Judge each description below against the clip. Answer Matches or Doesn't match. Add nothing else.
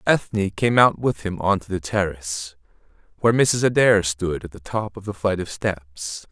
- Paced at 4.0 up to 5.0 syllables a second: Matches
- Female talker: Doesn't match